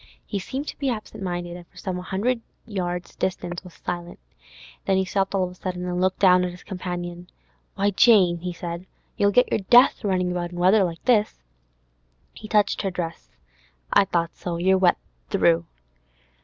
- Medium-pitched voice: Yes, medium, 180 Hz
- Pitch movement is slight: Yes, narrow, 2.2 semitones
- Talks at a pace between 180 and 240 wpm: Yes, average, 185 wpm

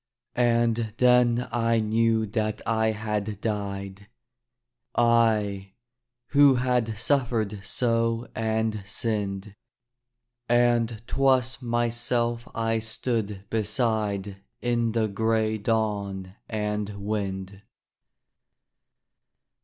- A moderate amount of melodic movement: No, narrow, 2.2 semitones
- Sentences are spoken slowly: Yes, slow, 85 wpm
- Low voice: Yes, low, 110 Hz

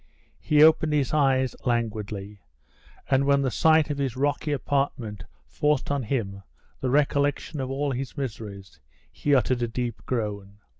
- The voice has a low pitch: Yes, low, 130 Hz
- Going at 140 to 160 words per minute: Yes, average, 150 wpm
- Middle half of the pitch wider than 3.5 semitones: Yes, average, 4.3 semitones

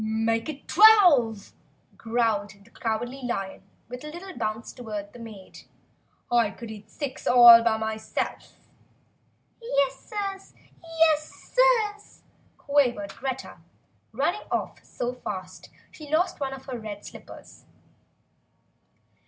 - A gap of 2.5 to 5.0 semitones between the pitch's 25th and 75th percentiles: No, wide, 5.6 semitones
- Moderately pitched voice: No, high, 245 Hz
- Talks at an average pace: No, slow, 120 wpm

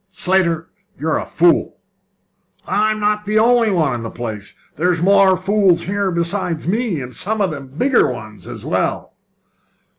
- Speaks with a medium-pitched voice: Yes, medium, 180 Hz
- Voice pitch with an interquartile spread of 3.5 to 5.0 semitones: Yes, average, 4.7 semitones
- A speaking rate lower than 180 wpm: Yes, average, 155 wpm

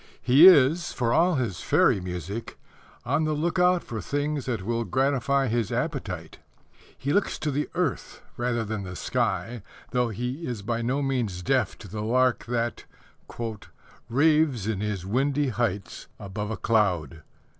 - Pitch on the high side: No, low, 120 Hz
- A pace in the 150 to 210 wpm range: Yes, average, 155 wpm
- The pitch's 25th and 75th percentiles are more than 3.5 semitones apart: Yes, average, 4.9 semitones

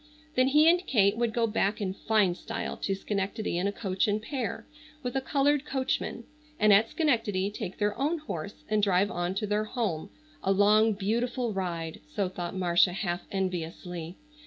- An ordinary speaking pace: Yes, average, 180 wpm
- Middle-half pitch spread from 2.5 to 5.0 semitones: Yes, average, 3.9 semitones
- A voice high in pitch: Yes, high, 205 Hz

